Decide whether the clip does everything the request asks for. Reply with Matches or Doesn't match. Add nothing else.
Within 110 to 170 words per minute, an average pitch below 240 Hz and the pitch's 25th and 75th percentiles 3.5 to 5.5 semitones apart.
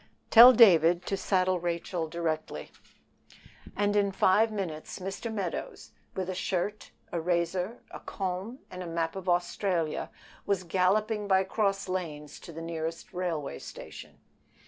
Doesn't match